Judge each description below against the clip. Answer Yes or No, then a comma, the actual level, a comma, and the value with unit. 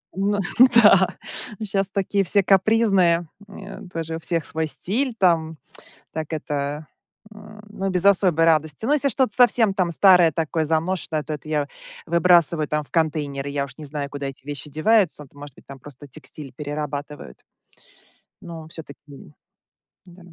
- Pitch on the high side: No, medium, 165 Hz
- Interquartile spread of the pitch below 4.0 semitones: No, average, 4.7 semitones